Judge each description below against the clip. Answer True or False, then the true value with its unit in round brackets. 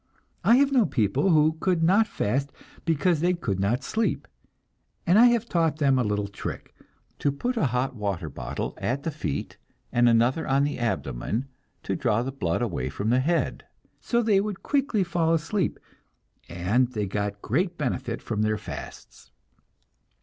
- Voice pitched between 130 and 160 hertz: True (135 Hz)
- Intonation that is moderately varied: False (8.3 semitones)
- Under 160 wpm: False (170 wpm)